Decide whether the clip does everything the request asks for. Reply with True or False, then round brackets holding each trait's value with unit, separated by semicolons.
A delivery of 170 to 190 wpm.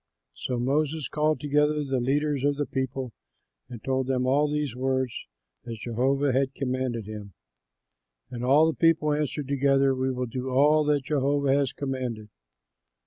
False (160 wpm)